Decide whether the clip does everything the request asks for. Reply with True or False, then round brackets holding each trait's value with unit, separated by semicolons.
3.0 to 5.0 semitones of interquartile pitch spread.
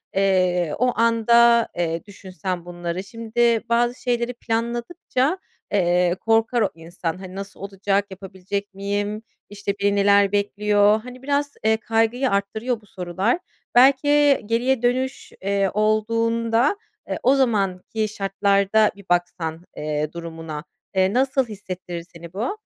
True (3.9 semitones)